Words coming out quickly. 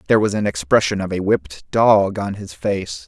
Yes: fast, 215 wpm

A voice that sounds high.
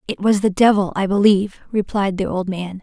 Yes: high, 195 Hz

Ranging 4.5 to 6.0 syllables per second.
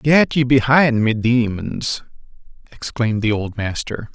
No: 4.1 syllables/s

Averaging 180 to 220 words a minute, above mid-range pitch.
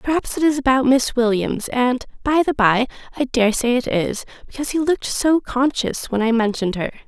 Yes: fast, 205 wpm; very high, 255 Hz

